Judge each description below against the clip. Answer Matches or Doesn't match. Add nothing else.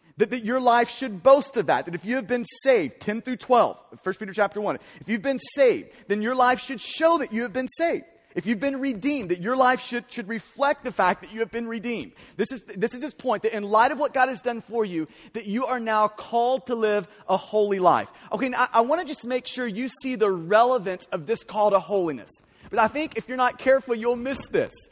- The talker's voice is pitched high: Matches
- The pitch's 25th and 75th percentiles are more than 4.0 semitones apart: Doesn't match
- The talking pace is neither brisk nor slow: Doesn't match